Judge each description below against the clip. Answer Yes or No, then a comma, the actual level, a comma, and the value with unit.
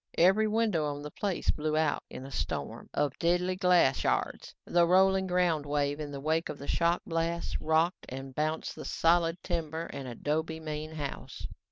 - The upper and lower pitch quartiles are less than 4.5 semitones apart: Yes, average, 2.9 semitones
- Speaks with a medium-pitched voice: Yes, medium, 160 Hz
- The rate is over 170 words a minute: Yes, average, 180 wpm